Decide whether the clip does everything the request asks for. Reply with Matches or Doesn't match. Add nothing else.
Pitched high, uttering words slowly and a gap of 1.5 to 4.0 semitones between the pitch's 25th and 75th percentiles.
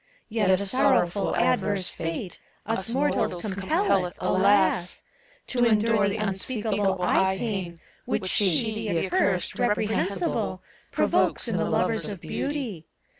Matches